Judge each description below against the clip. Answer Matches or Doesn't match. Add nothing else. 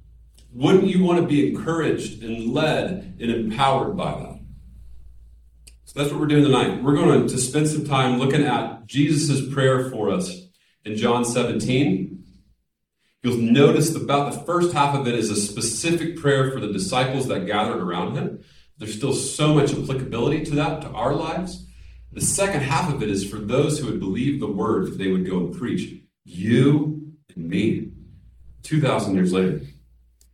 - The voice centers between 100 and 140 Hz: Matches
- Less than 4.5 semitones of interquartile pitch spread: Doesn't match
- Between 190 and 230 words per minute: Doesn't match